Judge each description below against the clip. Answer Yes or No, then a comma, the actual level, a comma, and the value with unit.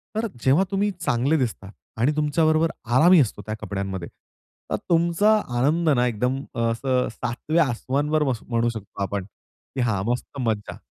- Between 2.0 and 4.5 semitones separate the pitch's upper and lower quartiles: No, wide, 5.4 semitones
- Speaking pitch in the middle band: No, low, 130 Hz